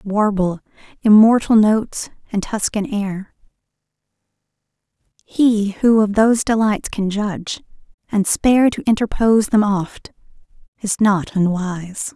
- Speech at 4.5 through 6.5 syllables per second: No, 4.3 syllables/s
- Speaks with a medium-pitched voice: No, high, 205 Hz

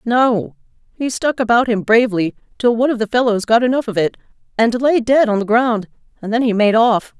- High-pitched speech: Yes, high, 230 Hz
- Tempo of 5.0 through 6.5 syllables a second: Yes, 5.5 syllables/s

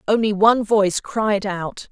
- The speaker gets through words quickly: No, average, 155 wpm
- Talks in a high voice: Yes, high, 210 Hz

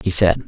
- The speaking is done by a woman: No, male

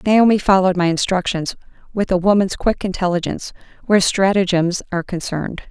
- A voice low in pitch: No, medium, 185 Hz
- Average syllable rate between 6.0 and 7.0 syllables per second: Yes, 6.1 syllables/s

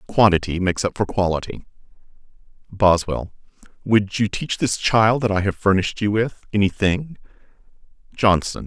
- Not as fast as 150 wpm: Yes, average, 140 wpm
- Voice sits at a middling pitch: No, low, 105 Hz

